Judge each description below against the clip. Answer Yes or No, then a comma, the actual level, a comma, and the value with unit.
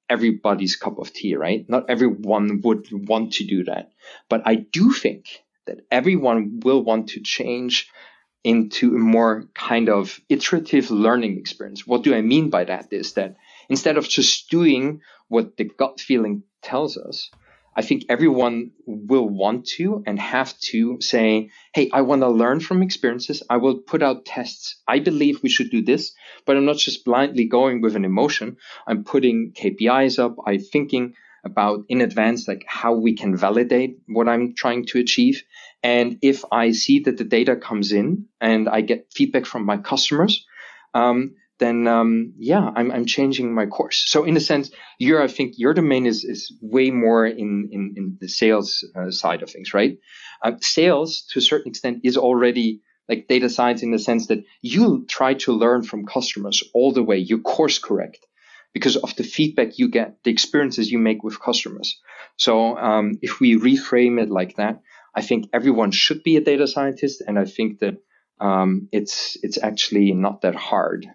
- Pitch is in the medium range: No, low, 120 Hz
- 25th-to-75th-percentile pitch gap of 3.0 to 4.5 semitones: Yes, average, 3.7 semitones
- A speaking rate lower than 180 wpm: No, average, 185 wpm